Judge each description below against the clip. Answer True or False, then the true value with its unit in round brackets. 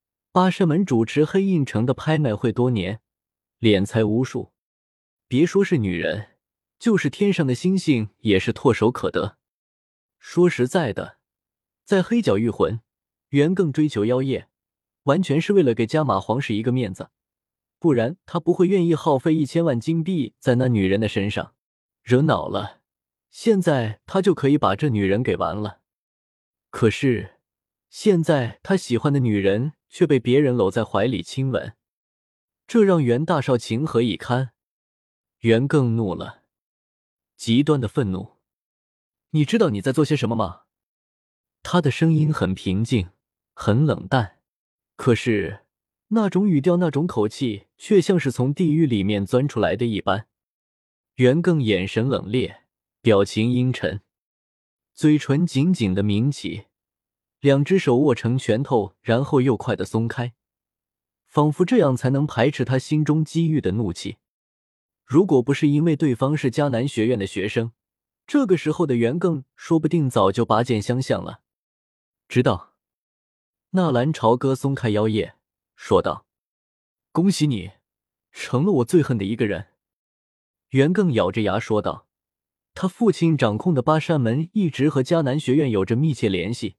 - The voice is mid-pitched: False (125 Hz)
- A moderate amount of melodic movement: False (6.5 semitones)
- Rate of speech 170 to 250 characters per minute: True (220 characters per minute)